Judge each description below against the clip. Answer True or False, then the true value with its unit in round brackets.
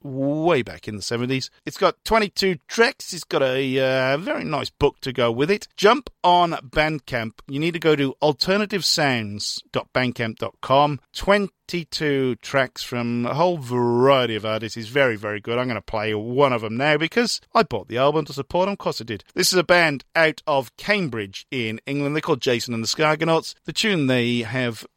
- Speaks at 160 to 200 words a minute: True (190 wpm)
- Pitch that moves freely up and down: True (5.9 semitones)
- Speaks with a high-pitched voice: False (140 Hz)